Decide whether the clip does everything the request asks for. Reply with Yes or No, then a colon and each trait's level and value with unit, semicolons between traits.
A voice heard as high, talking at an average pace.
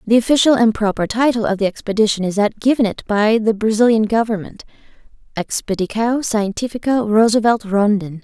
Yes: high, 220 Hz; average, 145 wpm